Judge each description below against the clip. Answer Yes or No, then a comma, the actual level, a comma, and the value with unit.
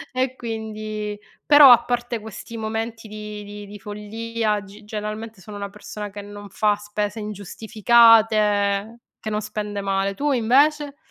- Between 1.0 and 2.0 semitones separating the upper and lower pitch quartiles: Yes, narrow, 1.7 semitones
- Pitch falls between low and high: No, high, 215 Hz